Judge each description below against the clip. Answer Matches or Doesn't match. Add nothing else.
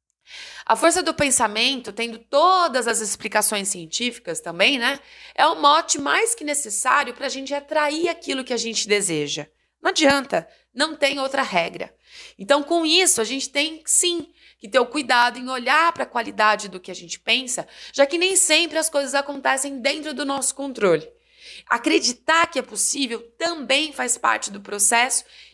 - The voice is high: Matches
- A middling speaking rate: Matches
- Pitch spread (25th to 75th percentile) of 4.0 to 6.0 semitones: Matches